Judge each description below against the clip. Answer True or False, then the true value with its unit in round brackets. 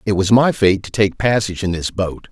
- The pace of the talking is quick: True (260 wpm)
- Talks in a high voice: False (100 Hz)